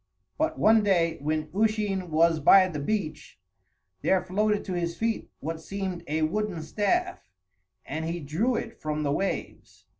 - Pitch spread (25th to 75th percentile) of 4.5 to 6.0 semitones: Yes, average, 5.0 semitones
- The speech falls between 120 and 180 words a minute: Yes, average, 155 wpm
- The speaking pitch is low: No, medium, 185 Hz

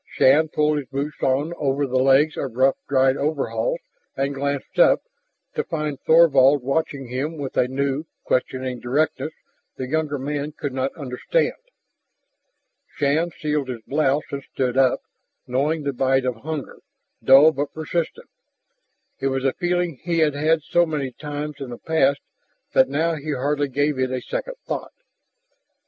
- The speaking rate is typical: Yes, average, 160 wpm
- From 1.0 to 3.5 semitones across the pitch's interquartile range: Yes, narrow, 2.6 semitones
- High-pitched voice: No, medium, 140 Hz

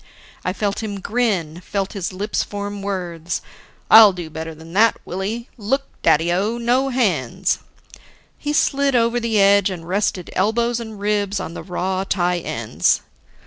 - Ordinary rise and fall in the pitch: Yes, average, 4.0 semitones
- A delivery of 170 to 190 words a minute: No, average, 155 wpm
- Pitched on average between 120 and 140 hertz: No, high, 200 Hz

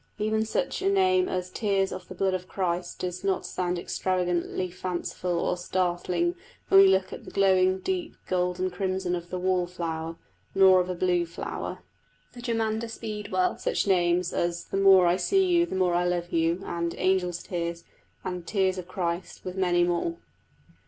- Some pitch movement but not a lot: No, narrow, 1.8 semitones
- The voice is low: No, medium, 185 Hz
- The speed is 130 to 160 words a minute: No, average, 180 wpm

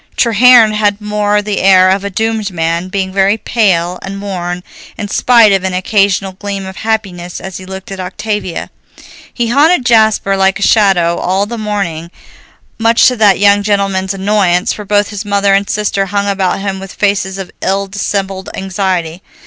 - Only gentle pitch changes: Yes, narrow, 1.8 semitones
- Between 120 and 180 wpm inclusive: Yes, average, 175 wpm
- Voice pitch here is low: No, high, 195 Hz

